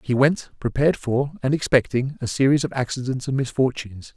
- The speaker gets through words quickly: No, average, 175 wpm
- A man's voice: Yes, male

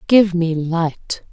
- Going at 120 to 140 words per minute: Yes, slow, 135 wpm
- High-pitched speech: No, medium, 175 Hz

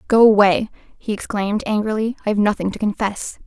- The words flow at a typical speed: Yes, average, 175 wpm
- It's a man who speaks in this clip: No, female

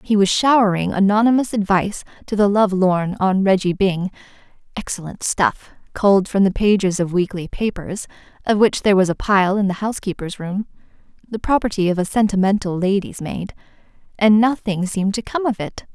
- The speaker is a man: No, female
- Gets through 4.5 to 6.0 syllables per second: Yes, 5.5 syllables/s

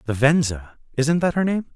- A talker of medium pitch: Yes, medium, 145 Hz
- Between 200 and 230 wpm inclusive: Yes, fast, 205 wpm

